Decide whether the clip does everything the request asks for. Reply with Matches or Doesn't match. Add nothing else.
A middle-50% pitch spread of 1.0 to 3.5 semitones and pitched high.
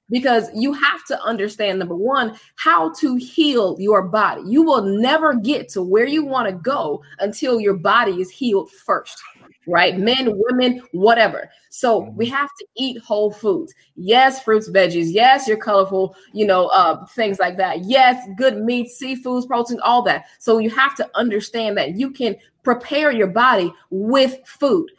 Doesn't match